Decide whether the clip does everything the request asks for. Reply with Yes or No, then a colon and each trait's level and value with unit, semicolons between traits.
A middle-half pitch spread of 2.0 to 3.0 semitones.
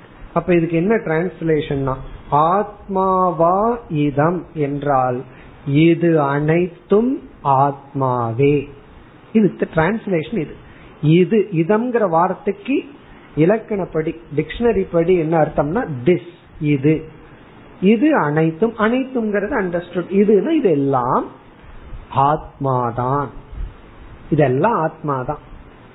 No: average, 5.3 semitones